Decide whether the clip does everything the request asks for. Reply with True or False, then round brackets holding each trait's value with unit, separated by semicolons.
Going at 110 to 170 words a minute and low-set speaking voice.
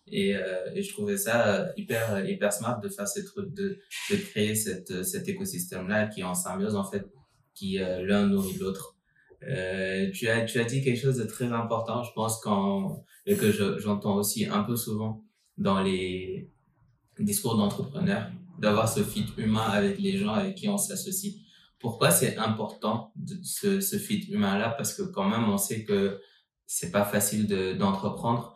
False (185 wpm; 125 Hz)